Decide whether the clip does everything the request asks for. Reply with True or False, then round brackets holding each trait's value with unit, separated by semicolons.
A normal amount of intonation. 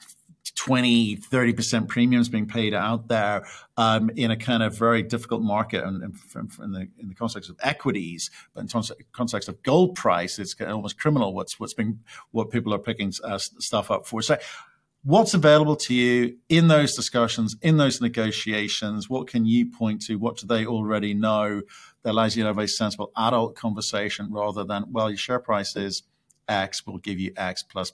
False (2.3 semitones)